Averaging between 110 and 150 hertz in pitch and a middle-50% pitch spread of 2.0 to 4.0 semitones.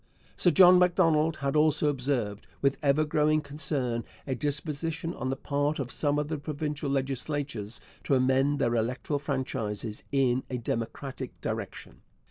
Yes: medium, 140 Hz; average, 2.8 semitones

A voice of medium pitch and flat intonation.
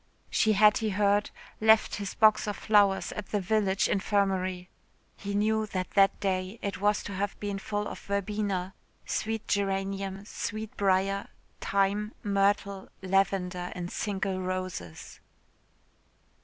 No: high, 200 Hz; narrow, 1.5 semitones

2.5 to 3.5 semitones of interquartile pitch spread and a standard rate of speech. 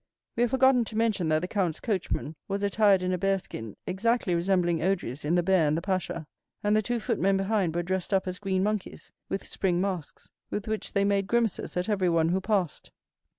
No: average, 2.8 semitones; fast, 210 wpm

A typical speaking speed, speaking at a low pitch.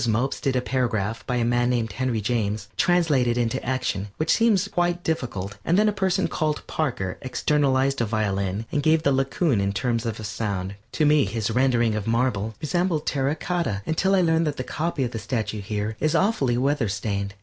Yes: average, 195 wpm; low, 125 Hz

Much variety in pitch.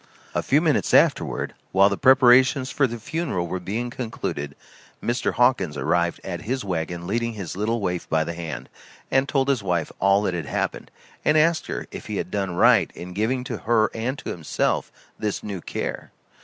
Yes: wide, 6.0 semitones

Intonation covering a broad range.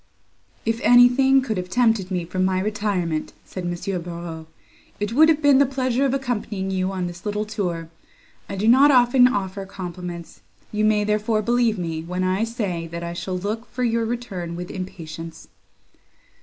No: average, 5.0 semitones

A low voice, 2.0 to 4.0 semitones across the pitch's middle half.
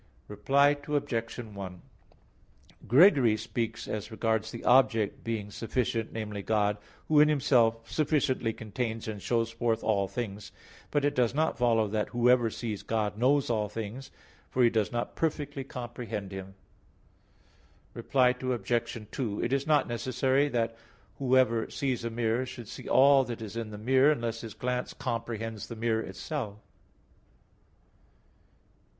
Yes: low, 115 Hz; average, 2.9 semitones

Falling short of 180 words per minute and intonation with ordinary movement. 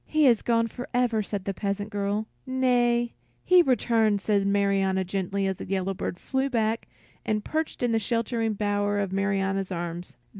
Yes: average, 165 wpm; average, 3.3 semitones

